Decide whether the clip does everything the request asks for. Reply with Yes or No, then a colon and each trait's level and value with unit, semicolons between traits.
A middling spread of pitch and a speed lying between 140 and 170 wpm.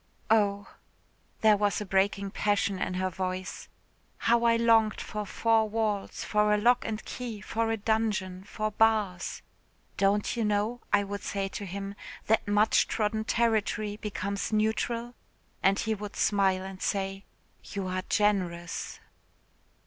No: narrow, 2.0 semitones; average, 145 wpm